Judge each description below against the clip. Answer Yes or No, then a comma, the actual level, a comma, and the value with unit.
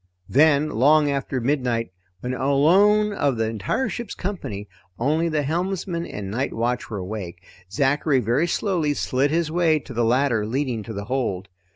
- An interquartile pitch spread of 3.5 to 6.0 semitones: Yes, wide, 5.4 semitones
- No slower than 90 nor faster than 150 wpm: No, average, 165 wpm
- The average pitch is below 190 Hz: Yes, low, 135 Hz